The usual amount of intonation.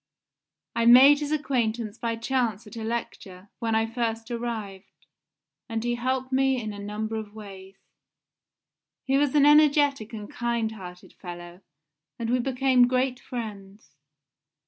Yes: average, 3.3 semitones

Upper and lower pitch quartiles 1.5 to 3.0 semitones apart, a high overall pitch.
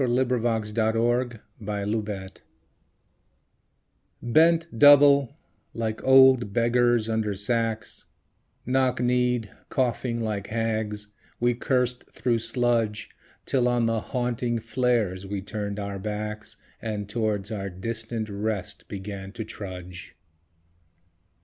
No: average, 2.7 semitones; low, 115 Hz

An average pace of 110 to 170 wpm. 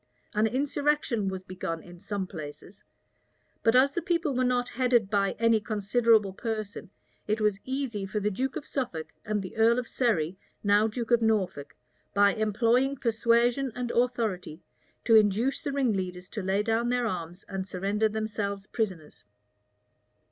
Yes: average, 155 wpm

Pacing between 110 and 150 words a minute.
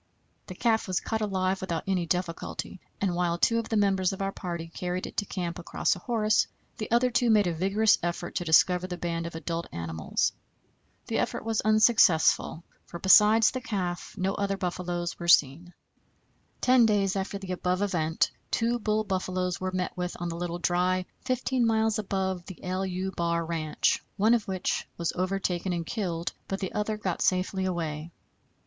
No: average, 180 wpm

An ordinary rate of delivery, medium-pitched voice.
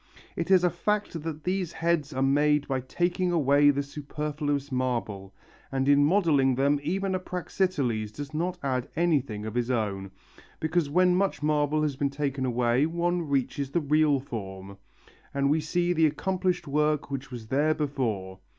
Yes: average, 170 wpm; medium, 145 Hz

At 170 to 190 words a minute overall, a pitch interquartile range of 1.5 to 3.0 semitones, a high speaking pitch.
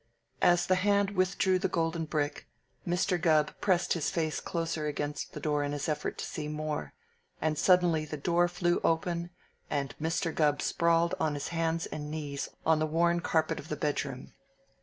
No: average, 180 wpm; narrow, 2.5 semitones; medium, 160 Hz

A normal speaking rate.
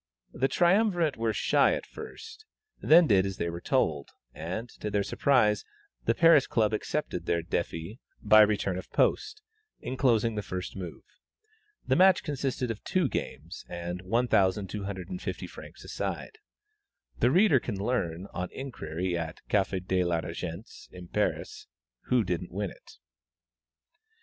Yes: average, 145 wpm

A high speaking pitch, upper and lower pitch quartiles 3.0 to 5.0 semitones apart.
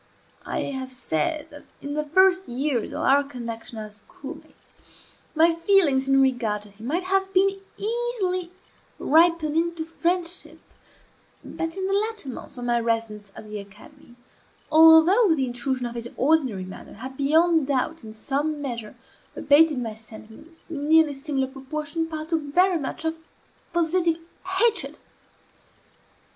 No: very high, 295 Hz; wide, 5.4 semitones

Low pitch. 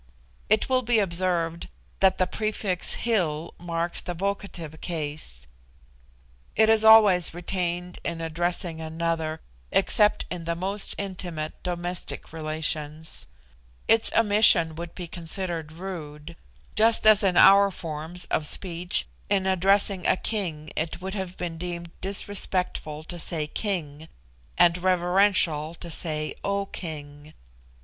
No: medium, 175 Hz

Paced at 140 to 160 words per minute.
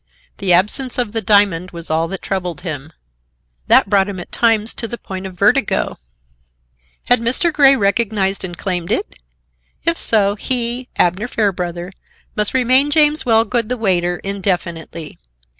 Yes: average, 150 wpm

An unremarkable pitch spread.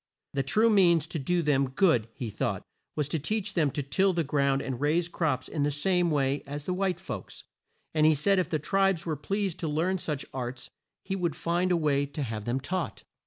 Yes: average, 4.5 semitones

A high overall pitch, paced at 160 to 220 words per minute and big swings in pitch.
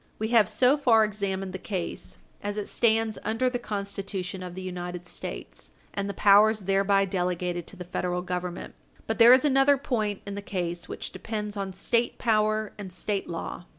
No: high, 200 Hz; average, 185 wpm; average, 3.1 semitones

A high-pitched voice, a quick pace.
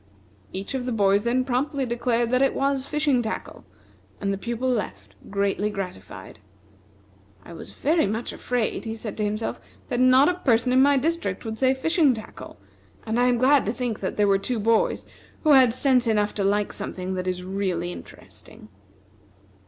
No: high, 235 Hz; average, 180 wpm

